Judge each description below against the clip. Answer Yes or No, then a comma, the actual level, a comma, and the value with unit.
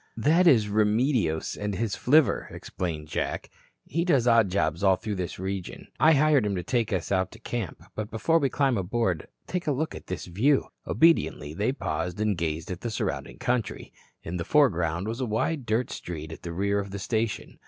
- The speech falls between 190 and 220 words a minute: Yes, average, 200 wpm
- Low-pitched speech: Yes, low, 105 Hz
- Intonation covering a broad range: Yes, wide, 5.9 semitones